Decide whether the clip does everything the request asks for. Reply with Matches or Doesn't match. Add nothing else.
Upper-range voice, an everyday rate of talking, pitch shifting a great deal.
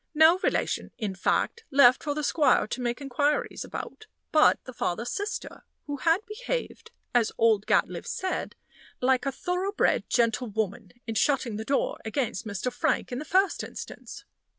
Matches